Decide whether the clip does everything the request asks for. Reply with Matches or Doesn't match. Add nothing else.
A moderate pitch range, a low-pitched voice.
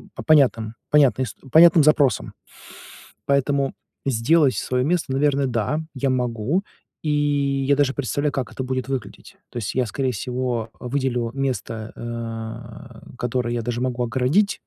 Matches